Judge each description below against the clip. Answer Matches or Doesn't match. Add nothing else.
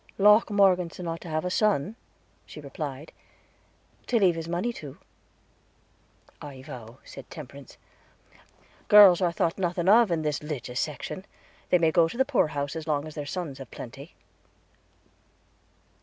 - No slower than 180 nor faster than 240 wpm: Doesn't match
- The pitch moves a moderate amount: Matches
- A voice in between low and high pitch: Matches